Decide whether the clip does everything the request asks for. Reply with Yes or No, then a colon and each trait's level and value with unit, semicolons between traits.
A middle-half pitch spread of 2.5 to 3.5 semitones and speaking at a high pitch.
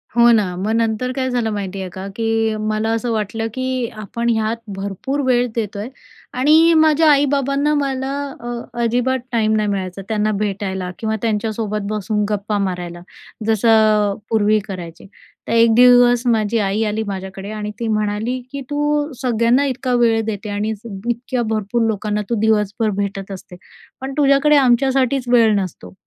Yes: average, 3.1 semitones; high, 220 Hz